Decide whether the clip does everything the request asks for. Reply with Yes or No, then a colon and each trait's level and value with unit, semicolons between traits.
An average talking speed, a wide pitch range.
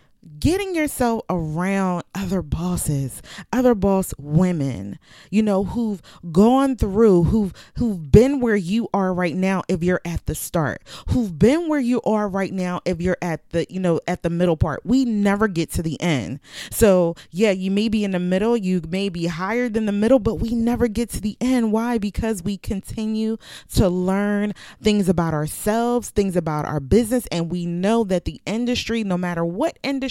No: average, 185 wpm; average, 4.3 semitones